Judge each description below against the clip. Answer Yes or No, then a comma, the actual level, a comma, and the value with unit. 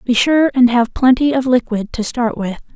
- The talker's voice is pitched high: Yes, high, 245 Hz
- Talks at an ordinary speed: No, fast, 220 wpm